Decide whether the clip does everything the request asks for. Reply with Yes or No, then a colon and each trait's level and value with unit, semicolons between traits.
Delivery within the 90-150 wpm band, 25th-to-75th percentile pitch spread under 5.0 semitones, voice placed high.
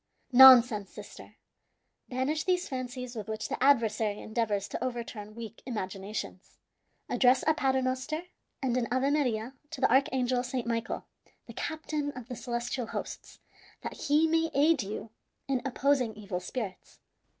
Yes: average, 140 wpm; average, 3.5 semitones; very high, 250 Hz